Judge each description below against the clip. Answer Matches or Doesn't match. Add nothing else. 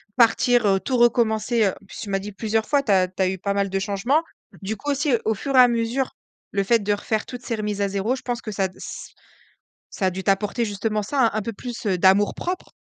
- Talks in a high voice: Matches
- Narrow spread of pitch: Doesn't match